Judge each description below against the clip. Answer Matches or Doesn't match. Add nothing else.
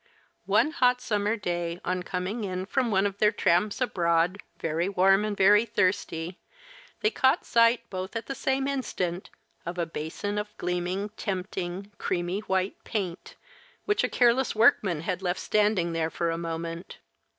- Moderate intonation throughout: Matches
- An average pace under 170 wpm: Matches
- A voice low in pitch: Doesn't match